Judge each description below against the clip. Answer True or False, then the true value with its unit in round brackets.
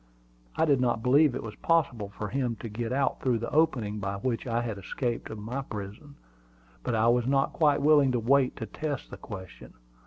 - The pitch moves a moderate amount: True (3.9 semitones)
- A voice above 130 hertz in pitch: False (120 Hz)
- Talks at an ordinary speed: False (210 wpm)